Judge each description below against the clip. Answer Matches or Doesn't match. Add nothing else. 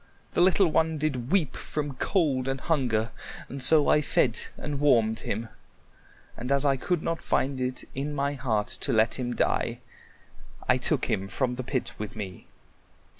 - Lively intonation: Doesn't match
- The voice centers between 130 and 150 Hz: Matches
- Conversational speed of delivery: Matches